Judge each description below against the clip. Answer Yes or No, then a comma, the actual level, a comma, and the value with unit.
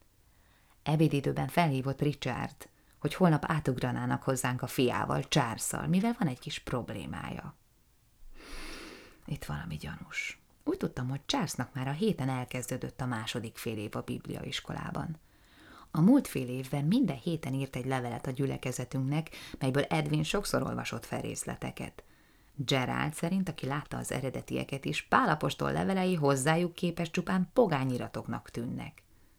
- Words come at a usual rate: Yes, average, 130 wpm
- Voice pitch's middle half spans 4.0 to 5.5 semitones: Yes, average, 4.6 semitones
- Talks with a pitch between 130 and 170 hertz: Yes, low, 135 Hz